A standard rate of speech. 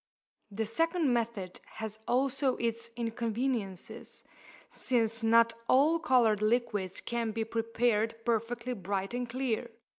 No: slow, 115 wpm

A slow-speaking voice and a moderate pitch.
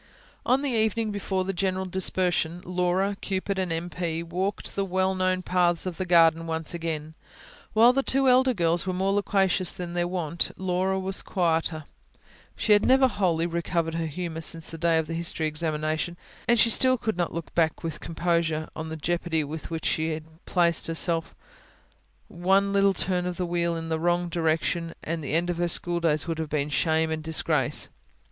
No: average, 190 wpm; medium, 175 Hz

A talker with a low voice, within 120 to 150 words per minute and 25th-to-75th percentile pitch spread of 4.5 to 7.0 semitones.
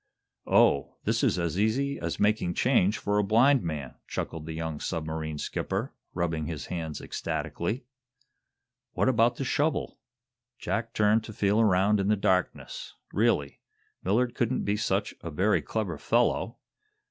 Yes: low, 100 Hz; average, 145 wpm; average, 5.2 semitones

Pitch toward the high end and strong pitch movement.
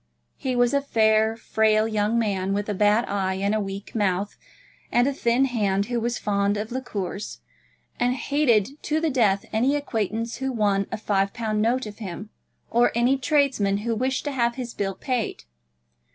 No: high, 220 Hz; average, 3.4 semitones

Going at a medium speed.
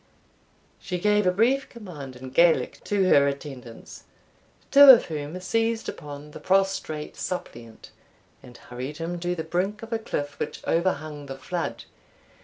Yes: average, 150 wpm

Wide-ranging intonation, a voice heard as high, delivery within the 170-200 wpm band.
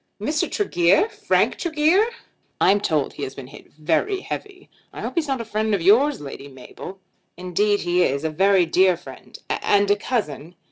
Yes: wide, 8.4 semitones; high, 195 Hz; average, 180 wpm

